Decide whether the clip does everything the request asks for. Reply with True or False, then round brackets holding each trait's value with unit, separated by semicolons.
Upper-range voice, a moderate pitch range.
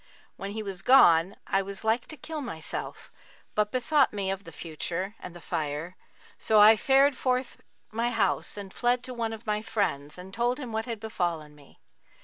True (210 Hz; 4.9 semitones)